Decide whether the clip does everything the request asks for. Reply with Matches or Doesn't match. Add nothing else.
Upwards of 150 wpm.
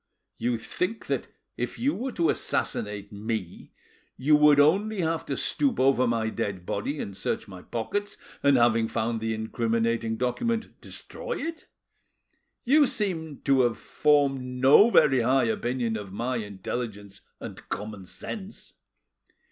Doesn't match